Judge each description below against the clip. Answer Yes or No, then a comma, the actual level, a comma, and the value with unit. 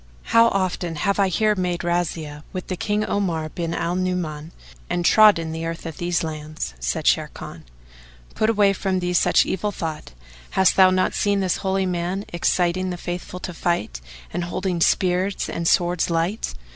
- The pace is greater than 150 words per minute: Yes, average, 170 wpm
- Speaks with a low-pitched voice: No, medium, 180 Hz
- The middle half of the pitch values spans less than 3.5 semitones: Yes, narrow, 2.4 semitones